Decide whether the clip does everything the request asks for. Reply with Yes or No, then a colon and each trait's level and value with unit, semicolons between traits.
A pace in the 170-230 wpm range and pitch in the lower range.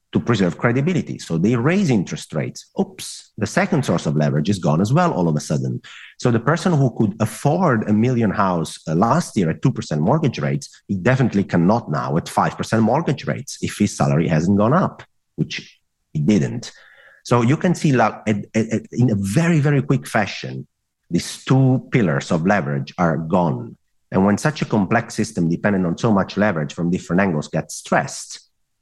Yes: average, 180 wpm; low, 110 Hz